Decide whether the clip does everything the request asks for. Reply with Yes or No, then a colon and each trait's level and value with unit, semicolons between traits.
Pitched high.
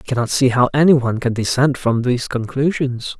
No: low, 125 Hz